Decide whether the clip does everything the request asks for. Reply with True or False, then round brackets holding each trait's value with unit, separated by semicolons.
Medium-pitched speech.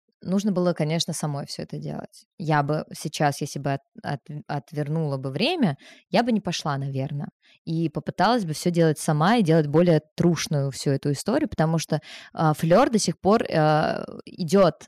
True (165 Hz)